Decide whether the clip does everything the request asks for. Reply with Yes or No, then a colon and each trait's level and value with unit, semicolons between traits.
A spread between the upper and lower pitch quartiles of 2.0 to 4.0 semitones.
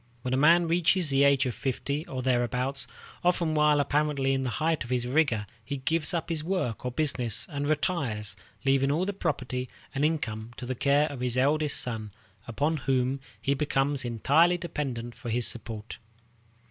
Yes: average, 3.6 semitones